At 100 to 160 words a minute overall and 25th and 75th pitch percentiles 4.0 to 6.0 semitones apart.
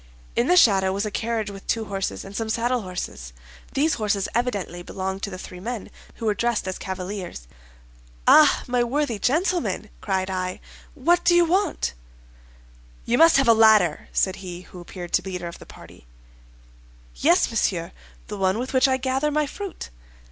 No: average, 180 wpm; wide, 5.5 semitones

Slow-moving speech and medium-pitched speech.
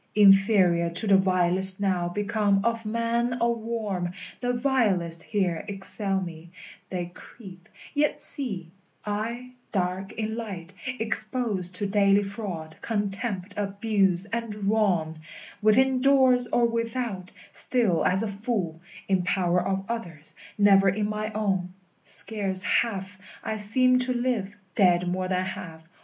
No: slow, 130 wpm; high, 200 Hz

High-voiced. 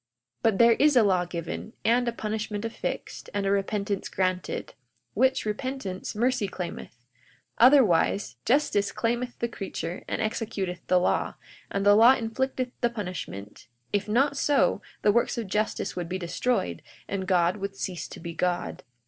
Yes: high, 205 Hz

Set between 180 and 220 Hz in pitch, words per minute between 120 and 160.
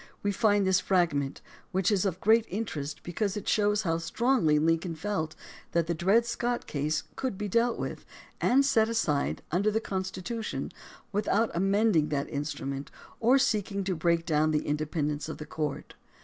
No: medium, 185 Hz; average, 170 wpm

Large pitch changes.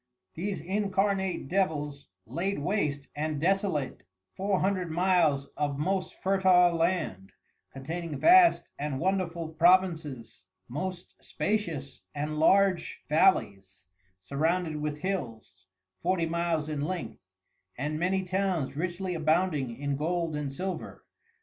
No: average, 4.3 semitones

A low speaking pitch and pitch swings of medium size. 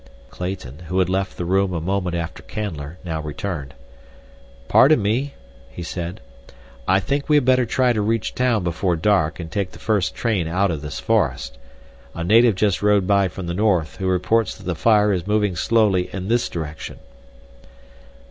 Yes: very low, 95 Hz; average, 3.9 semitones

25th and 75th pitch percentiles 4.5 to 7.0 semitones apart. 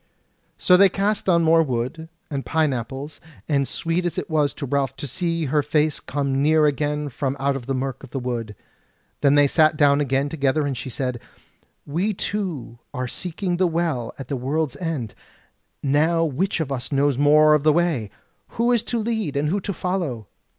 No: average, 3.5 semitones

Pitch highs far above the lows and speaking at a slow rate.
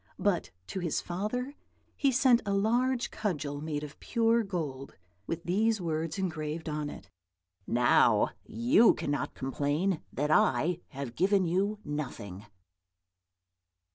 Yes: wide, 5.9 semitones; slow, 125 wpm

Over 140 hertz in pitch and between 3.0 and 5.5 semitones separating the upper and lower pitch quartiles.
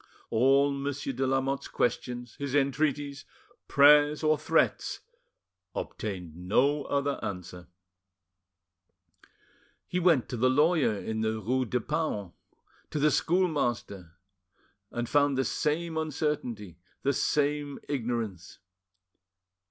No: low, 135 Hz; average, 4.2 semitones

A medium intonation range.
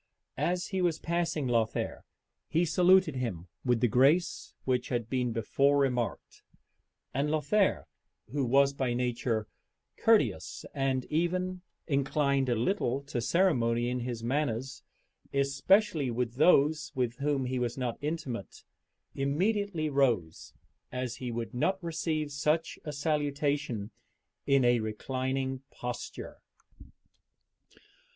Yes: average, 4.0 semitones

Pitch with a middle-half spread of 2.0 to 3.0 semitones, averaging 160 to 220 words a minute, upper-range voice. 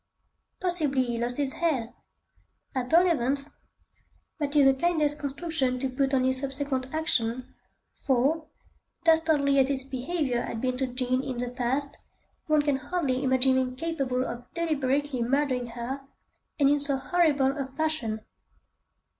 No: narrow, 2.6 semitones; average, 145 wpm; very high, 270 Hz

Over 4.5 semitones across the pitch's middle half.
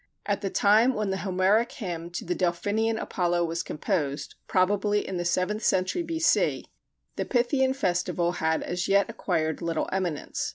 No: average, 3.5 semitones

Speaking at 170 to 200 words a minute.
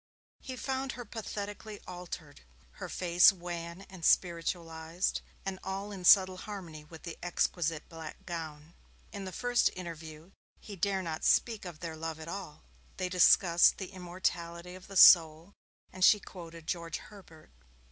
No: average, 155 wpm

